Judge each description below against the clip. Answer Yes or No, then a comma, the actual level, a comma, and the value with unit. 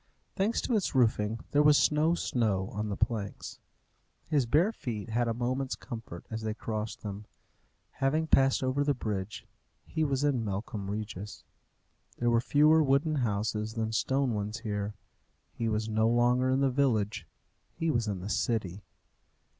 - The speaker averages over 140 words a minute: Yes, average, 160 wpm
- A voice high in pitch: No, low, 115 Hz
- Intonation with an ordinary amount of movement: Yes, average, 4.3 semitones